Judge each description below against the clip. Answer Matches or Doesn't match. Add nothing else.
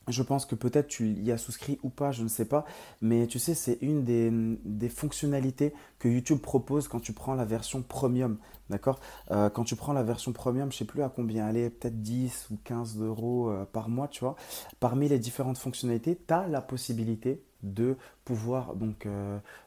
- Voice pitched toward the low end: Matches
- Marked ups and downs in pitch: Doesn't match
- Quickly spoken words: Doesn't match